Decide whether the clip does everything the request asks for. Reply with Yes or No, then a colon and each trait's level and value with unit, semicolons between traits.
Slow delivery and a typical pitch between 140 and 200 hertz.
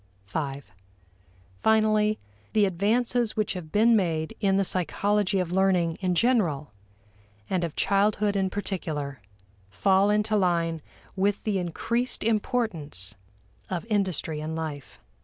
Yes: slow, 120 wpm; high, 190 Hz